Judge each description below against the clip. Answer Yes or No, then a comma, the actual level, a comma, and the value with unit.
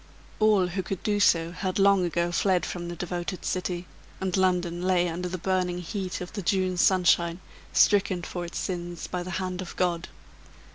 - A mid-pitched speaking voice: Yes, medium, 180 Hz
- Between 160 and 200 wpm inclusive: Yes, average, 185 wpm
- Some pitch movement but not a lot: No, narrow, 1.4 semitones